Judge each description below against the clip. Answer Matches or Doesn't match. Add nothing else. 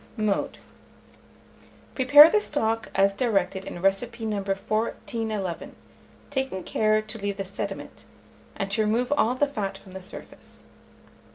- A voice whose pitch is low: Doesn't match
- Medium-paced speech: Doesn't match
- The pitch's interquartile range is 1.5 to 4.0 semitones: Matches